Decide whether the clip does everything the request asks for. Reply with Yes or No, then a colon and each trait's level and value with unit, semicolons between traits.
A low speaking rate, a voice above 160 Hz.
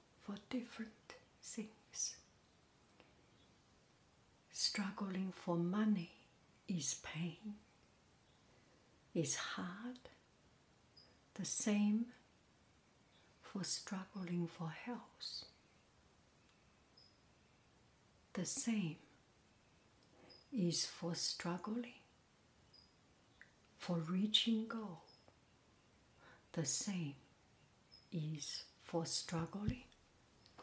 Yes: slow, 55 wpm; high, 190 Hz